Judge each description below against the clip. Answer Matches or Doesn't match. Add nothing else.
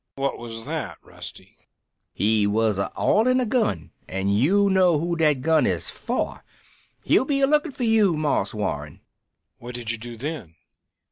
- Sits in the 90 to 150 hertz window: Matches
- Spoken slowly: Doesn't match